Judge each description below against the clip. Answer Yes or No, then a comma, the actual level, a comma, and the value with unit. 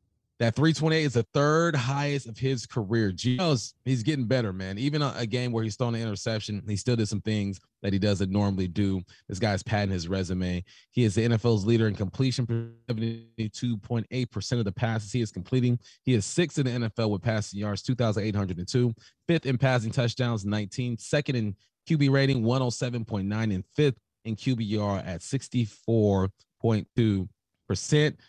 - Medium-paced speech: Yes, average, 170 wpm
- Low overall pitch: Yes, low, 115 Hz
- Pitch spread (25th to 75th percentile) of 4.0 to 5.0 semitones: No, average, 3.6 semitones